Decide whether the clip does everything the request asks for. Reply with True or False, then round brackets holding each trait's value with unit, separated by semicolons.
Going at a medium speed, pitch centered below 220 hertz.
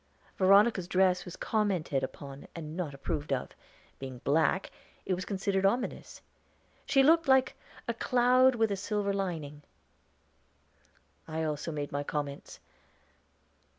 False (125 wpm; 185 Hz)